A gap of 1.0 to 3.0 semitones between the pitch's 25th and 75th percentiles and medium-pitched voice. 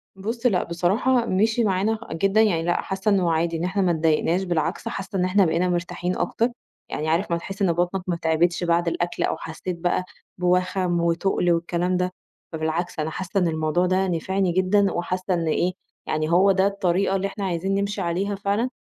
Yes: narrow, 2.4 semitones; medium, 180 Hz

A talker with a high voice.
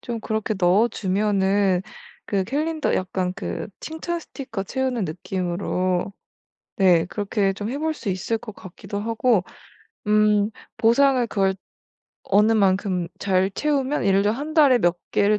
Yes: high, 205 Hz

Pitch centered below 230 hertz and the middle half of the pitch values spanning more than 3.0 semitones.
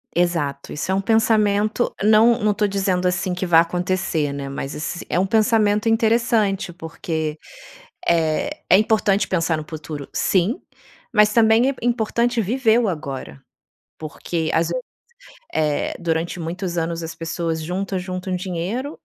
Yes: medium, 185 Hz; average, 4.7 semitones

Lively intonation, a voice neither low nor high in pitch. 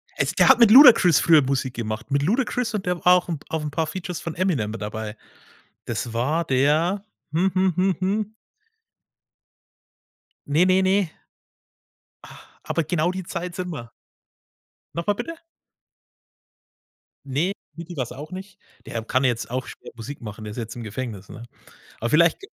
Yes: wide, 6.7 semitones; medium, 160 Hz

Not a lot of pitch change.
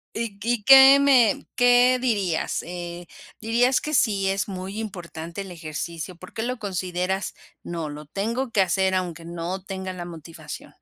No: average, 4.7 semitones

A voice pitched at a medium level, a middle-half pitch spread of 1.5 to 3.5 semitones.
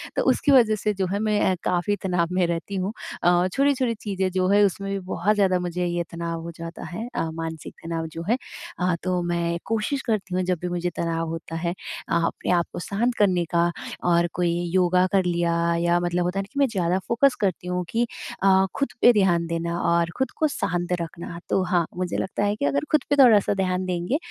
Yes: medium, 180 Hz; average, 2.9 semitones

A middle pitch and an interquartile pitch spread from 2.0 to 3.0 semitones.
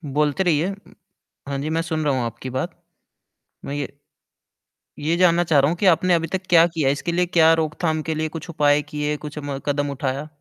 Yes: medium, 155 Hz; narrow, 2.5 semitones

